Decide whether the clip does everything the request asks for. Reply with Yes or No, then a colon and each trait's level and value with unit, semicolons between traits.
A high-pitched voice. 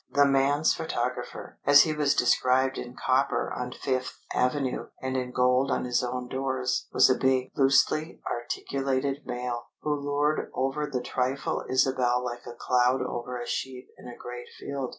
No: low, 130 Hz